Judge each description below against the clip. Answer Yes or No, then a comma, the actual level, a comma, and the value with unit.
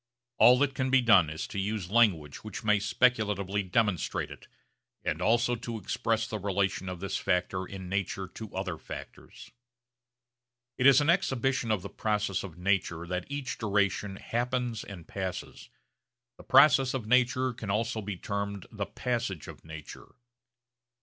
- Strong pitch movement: No, average, 3.9 semitones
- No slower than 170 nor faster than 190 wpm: No, average, 155 wpm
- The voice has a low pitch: Yes, low, 105 Hz